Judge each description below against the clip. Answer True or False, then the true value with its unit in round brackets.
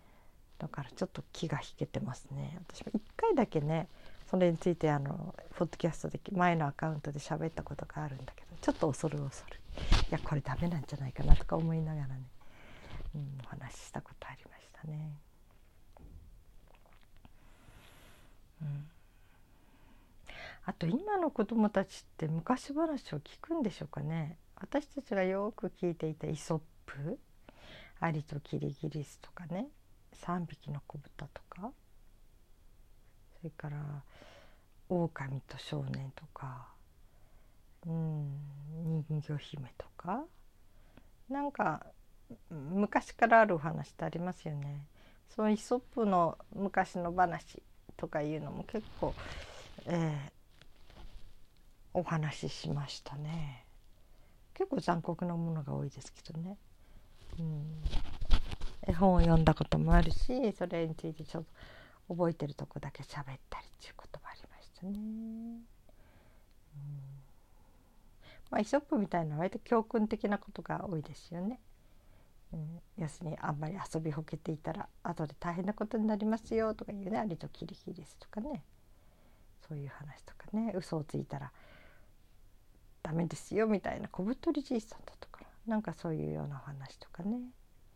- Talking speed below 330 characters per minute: True (280 characters per minute)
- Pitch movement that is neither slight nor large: False (6.2 semitones)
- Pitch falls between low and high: True (155 Hz)